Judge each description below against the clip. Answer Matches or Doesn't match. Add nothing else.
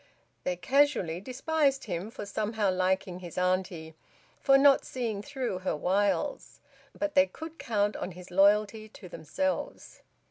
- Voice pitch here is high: Matches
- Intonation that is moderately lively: Doesn't match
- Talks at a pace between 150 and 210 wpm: Doesn't match